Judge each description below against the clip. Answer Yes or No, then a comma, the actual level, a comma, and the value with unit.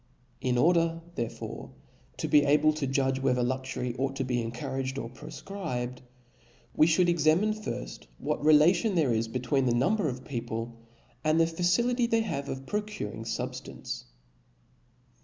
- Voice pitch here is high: No, medium, 140 Hz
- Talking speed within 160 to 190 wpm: No, average, 150 wpm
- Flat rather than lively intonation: No, average, 5.3 semitones